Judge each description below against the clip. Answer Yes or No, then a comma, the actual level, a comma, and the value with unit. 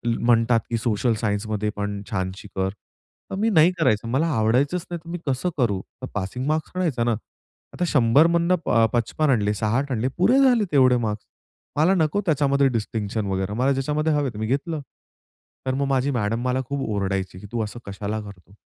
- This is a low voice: Yes, low, 125 Hz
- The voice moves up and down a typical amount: No, wide, 5.8 semitones